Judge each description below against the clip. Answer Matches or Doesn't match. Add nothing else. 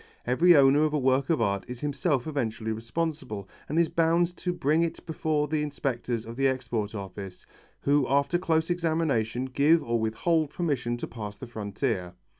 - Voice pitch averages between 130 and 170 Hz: Matches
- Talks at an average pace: Matches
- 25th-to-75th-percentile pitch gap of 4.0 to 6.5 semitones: Matches